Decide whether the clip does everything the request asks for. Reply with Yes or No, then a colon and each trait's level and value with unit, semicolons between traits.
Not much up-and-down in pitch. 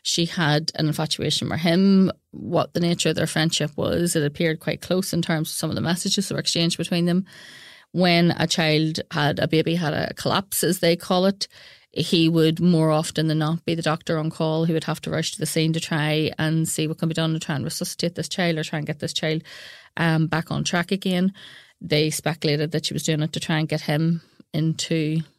Yes: narrow, 1.6 semitones